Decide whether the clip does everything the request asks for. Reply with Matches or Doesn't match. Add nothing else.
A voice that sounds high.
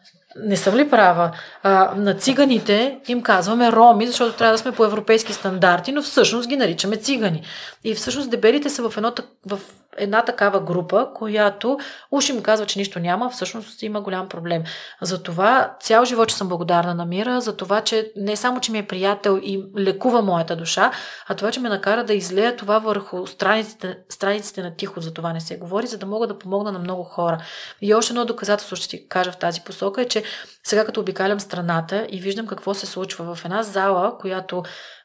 Matches